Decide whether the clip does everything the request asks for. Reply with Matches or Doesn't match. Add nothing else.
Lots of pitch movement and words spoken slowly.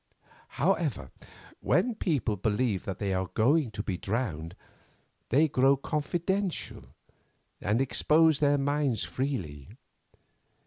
Matches